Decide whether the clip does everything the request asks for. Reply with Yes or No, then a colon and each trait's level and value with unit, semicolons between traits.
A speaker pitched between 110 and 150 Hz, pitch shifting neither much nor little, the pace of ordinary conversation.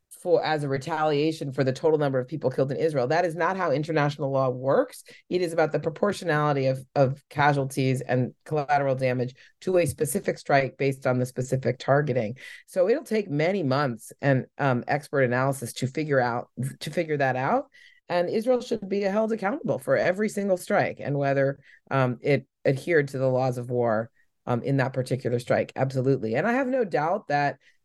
Yes: medium, 140 Hz; average, 3.9 semitones; average, 185 wpm